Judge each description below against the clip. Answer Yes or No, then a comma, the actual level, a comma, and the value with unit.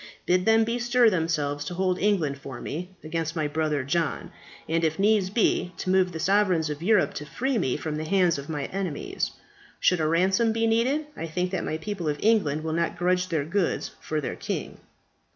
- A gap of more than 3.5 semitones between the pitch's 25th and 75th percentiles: Yes, average, 4.4 semitones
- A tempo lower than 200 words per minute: No, fast, 205 wpm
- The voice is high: No, medium, 175 Hz